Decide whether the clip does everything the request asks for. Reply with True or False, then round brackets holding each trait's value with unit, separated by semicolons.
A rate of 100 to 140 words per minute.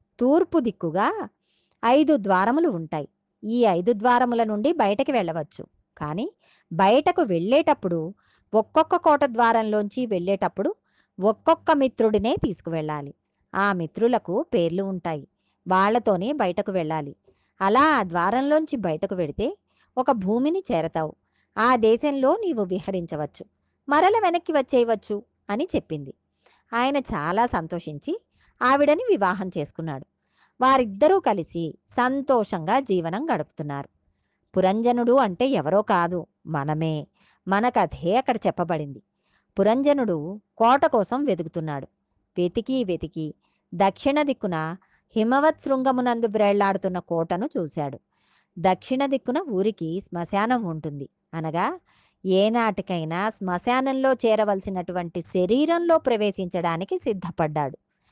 False (90 wpm)